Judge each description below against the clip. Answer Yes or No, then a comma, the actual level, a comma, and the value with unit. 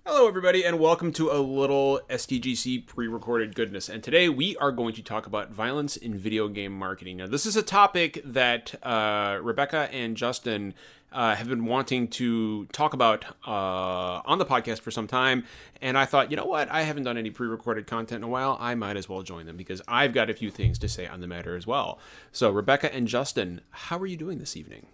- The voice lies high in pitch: No, low, 120 Hz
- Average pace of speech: No, fast, 225 wpm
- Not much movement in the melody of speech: No, average, 4.5 semitones